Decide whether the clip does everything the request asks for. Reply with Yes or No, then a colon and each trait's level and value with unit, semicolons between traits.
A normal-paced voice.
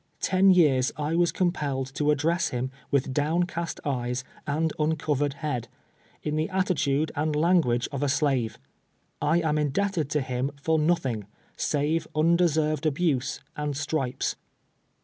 Yes: average, 150 wpm